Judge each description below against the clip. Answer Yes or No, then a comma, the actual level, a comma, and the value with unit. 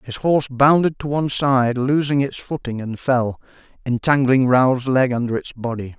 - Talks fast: No, average, 170 wpm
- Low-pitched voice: Yes, low, 130 Hz